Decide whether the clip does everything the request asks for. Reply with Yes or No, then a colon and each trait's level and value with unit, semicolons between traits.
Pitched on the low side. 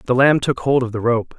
Yes: low, 125 Hz